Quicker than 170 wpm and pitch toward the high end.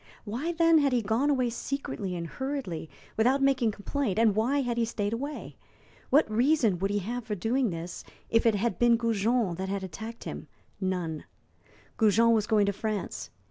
Yes: average, 180 wpm; high, 225 Hz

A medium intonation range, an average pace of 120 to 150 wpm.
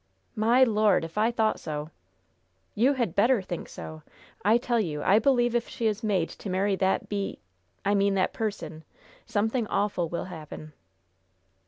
No: average, 3.8 semitones; average, 165 wpm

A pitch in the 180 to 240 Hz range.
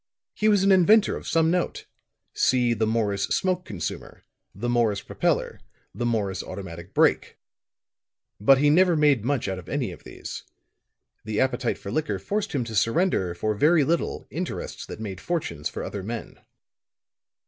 No: low, 120 Hz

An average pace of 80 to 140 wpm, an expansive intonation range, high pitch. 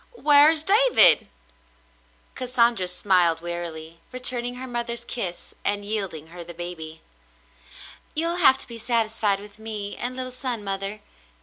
Yes: slow, 135 wpm; wide, 5.9 semitones; high, 220 Hz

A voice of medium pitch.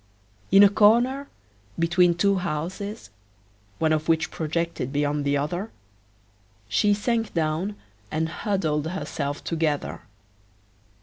Yes: medium, 170 Hz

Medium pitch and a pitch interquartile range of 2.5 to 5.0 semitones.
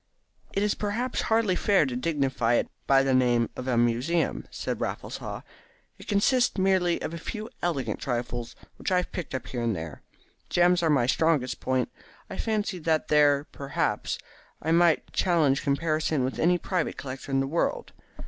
No: medium, 155 Hz; wide, 5.6 semitones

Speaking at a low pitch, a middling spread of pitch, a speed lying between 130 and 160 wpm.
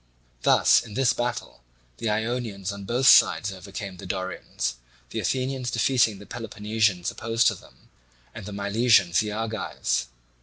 Yes: low, 105 Hz; average, 3.1 semitones; average, 145 wpm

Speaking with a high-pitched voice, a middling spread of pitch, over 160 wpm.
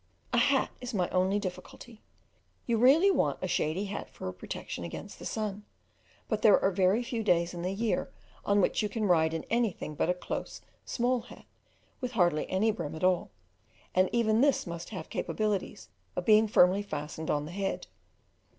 Yes: high, 195 Hz; average, 4.1 semitones; average, 185 wpm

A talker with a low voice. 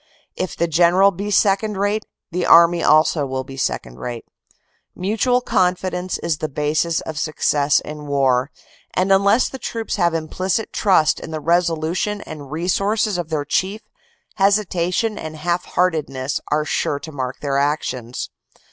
No: medium, 170 Hz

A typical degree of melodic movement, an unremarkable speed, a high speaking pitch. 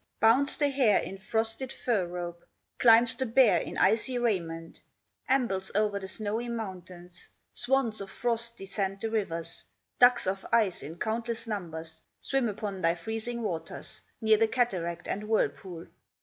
Yes: average, 4.0 semitones; average, 150 wpm; high, 215 Hz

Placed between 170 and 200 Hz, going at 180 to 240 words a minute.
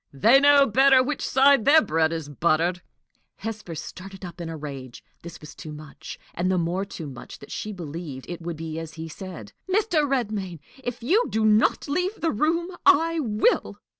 Yes: high, 190 Hz; average, 190 wpm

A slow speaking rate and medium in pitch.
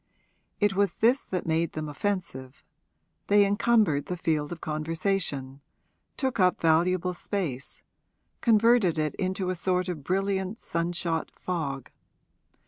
Yes: slow, 130 wpm; medium, 180 Hz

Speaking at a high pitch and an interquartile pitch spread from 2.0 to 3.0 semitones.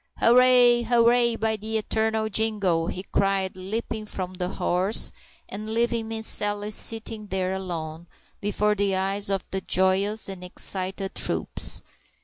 Yes: high, 205 Hz; average, 2.7 semitones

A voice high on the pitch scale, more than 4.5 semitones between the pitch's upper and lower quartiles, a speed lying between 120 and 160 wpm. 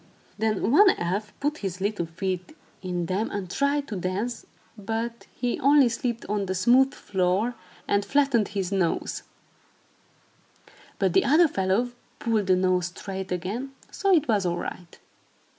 Yes: high, 205 Hz; average, 4.9 semitones; average, 150 wpm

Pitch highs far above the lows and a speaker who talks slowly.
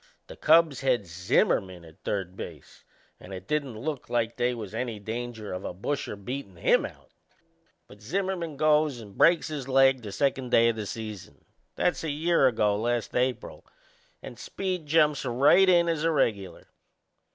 No: wide, 6.3 semitones; average, 170 wpm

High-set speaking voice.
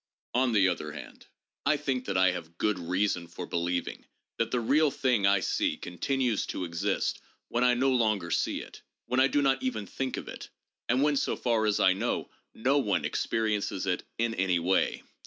No: low, 110 Hz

